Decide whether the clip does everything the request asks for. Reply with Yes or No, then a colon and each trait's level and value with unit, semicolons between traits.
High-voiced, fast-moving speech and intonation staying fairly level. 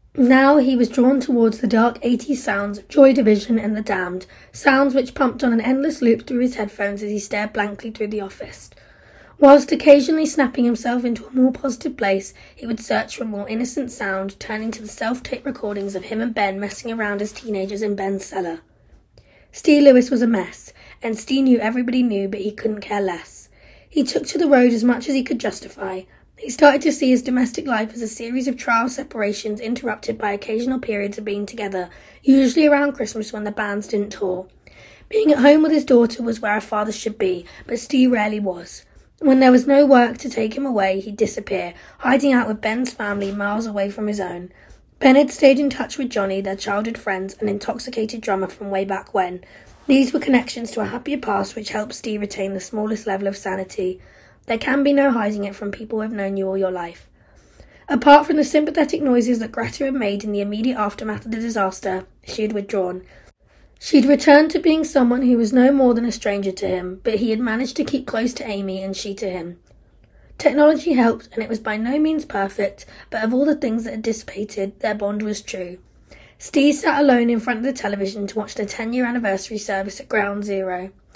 No: high, 225 Hz; fast, 215 wpm; average, 4.5 semitones